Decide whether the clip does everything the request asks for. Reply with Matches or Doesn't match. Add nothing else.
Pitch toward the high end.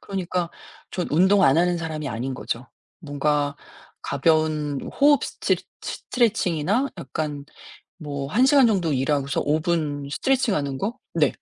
Doesn't match